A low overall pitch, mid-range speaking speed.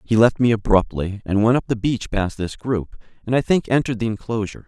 No: low, 110 Hz; fast, 230 wpm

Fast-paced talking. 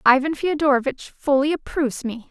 No: slow, 130 wpm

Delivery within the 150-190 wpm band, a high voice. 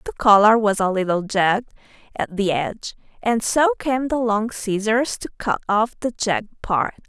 Yes: average, 180 wpm; high, 215 Hz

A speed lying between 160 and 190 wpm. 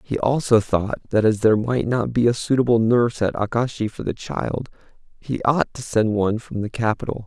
No: fast, 205 wpm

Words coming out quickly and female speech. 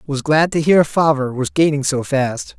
No: fast, 210 wpm; male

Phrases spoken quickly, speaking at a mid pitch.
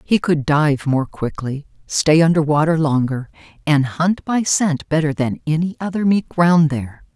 No: average, 170 wpm; medium, 155 Hz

